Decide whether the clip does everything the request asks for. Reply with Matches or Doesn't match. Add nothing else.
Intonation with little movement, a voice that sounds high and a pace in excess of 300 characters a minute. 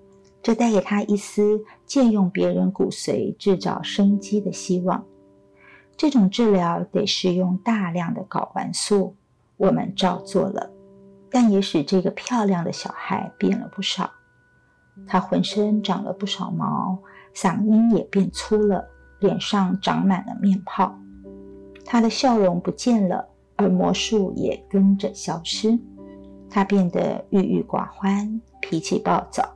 Doesn't match